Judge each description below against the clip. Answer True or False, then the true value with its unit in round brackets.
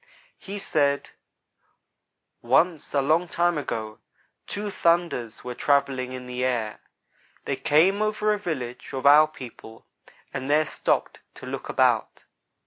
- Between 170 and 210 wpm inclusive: False (135 wpm)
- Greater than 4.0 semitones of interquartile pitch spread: True (5.5 semitones)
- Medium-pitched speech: True (145 Hz)